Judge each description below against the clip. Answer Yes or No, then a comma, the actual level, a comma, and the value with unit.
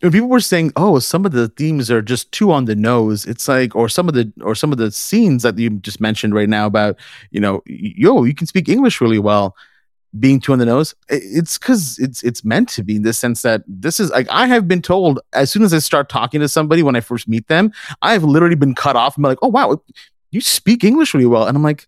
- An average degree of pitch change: No, wide, 7.0 semitones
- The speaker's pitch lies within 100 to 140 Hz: Yes, low, 135 Hz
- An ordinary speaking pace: No, fast, 265 wpm